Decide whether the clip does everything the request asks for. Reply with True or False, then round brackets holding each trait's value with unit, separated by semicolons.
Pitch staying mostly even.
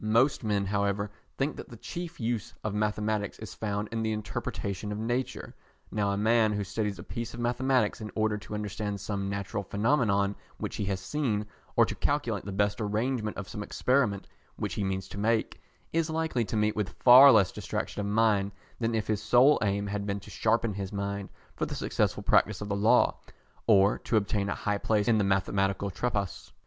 True (2.2 semitones)